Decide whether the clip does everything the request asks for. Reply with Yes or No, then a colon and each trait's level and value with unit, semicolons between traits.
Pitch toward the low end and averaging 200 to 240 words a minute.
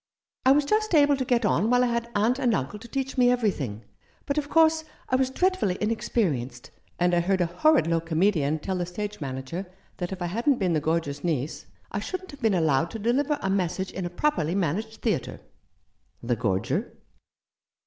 No: high, 200 Hz; fast, 205 wpm